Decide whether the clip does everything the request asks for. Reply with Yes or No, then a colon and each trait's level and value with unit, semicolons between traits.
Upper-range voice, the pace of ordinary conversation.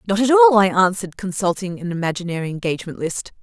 Yes: high, 195 Hz; average, 175 wpm